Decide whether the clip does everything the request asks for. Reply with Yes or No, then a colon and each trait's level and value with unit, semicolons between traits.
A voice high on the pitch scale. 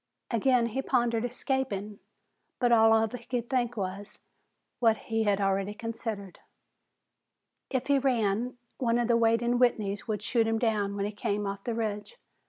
Yes: high, 225 Hz